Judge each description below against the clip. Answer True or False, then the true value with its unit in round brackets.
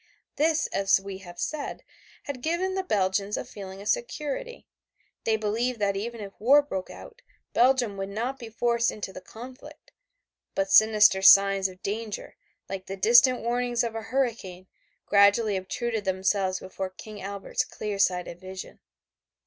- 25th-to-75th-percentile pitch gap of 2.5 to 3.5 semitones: False (3.9 semitones)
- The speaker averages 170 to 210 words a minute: False (155 wpm)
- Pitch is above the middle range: True (210 Hz)